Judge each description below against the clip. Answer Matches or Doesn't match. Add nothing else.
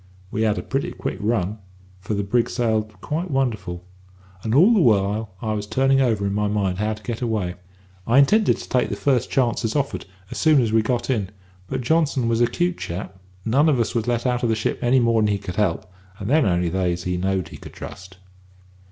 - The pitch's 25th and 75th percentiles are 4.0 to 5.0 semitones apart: Matches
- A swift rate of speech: Matches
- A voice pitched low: Matches